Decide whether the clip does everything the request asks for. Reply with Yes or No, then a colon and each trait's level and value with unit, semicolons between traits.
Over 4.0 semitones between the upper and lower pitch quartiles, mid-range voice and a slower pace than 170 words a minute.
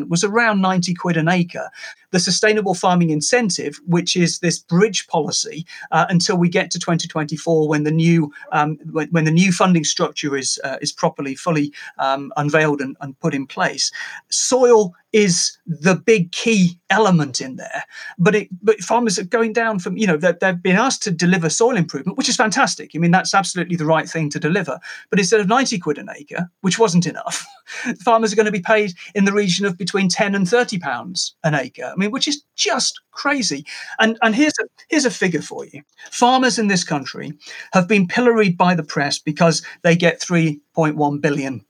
No: average, 5.2 semitones; medium, 180 Hz; average, 195 wpm